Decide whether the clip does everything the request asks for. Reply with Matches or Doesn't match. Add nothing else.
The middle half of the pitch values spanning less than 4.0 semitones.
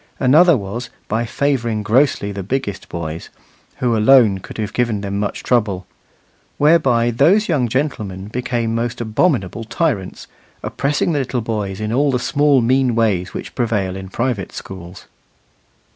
Doesn't match